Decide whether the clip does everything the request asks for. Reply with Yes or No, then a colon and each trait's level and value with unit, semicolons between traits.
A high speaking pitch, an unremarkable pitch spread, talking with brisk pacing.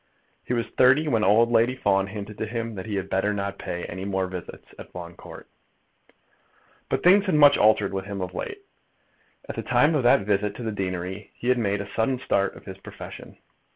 No: low, 105 Hz; average, 3.7 semitones; fast, 215 wpm